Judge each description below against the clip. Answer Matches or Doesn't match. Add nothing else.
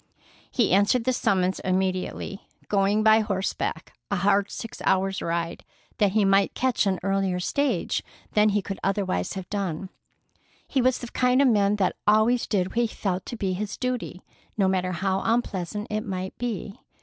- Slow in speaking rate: Doesn't match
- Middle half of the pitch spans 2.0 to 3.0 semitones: Matches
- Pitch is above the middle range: Matches